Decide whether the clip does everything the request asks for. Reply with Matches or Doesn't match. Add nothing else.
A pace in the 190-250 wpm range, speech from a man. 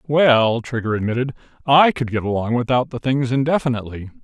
Doesn't match